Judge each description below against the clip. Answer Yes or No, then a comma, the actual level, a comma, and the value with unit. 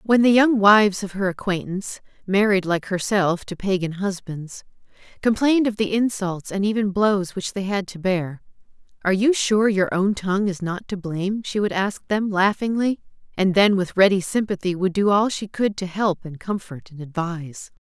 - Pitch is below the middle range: No, high, 195 Hz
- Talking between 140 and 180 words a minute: No, average, 190 wpm